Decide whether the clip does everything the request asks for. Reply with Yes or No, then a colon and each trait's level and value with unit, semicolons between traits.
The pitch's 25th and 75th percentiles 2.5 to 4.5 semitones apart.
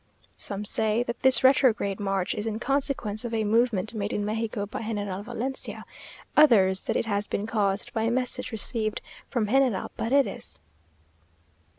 Yes: average, 3.0 semitones